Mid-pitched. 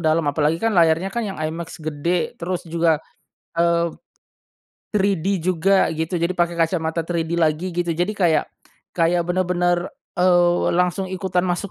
Yes: medium, 175 Hz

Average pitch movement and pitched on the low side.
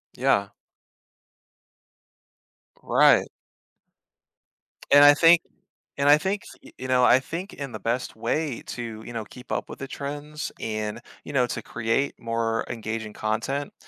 Yes: average, 4.2 semitones; low, 125 Hz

